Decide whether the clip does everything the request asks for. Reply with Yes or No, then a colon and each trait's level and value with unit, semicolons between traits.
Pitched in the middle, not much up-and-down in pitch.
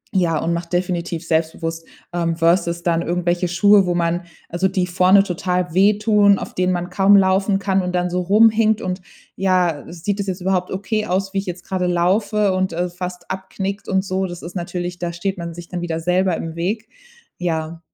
Yes: medium, 180 Hz; narrow, 1.9 semitones